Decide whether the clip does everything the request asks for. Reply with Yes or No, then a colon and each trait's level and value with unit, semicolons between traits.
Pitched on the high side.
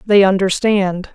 Yes: high, 195 Hz